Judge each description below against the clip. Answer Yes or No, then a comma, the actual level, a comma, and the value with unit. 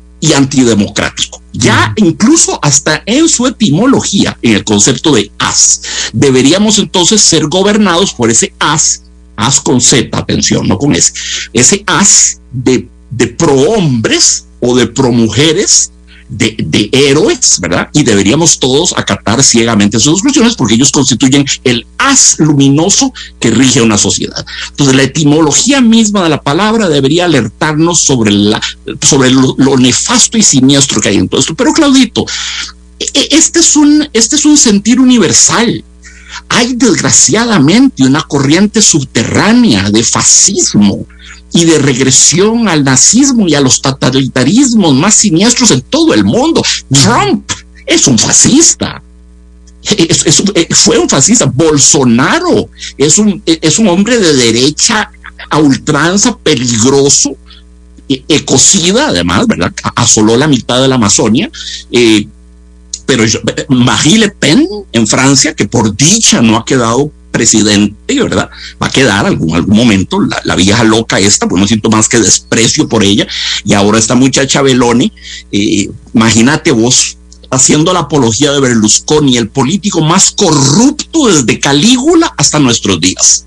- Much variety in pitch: Yes, wide, 8.7 semitones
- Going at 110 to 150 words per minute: Yes, average, 140 wpm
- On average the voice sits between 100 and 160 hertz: Yes, low, 135 Hz